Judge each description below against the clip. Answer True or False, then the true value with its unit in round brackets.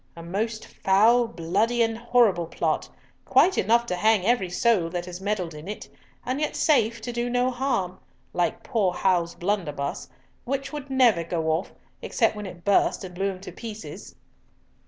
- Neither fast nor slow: True (170 wpm)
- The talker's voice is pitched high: True (210 Hz)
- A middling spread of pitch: True (5.0 semitones)